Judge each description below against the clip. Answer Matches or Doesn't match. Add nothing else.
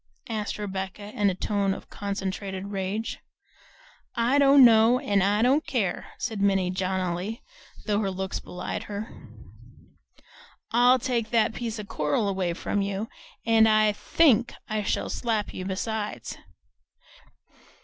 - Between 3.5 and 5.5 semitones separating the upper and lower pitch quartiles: Doesn't match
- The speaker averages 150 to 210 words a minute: Doesn't match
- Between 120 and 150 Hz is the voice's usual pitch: Doesn't match